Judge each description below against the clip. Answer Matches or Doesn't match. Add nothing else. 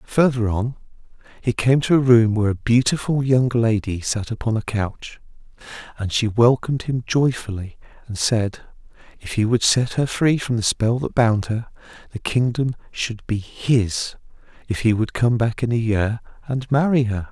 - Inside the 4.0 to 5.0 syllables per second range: Matches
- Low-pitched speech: Matches